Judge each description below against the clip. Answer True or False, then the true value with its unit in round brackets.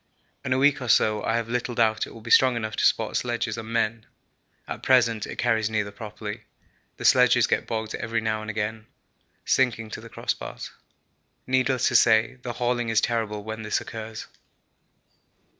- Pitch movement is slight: True (1.7 semitones)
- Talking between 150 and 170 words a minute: False (180 wpm)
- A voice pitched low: True (115 Hz)